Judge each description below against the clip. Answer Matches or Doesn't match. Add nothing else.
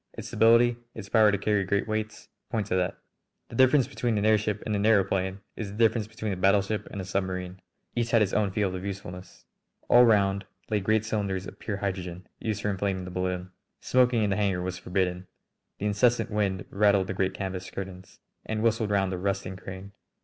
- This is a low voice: Matches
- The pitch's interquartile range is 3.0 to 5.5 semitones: Doesn't match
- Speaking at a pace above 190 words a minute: Matches